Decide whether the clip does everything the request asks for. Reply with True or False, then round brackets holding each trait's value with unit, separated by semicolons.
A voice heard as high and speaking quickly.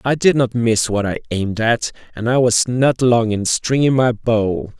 False (120 Hz; 215 wpm)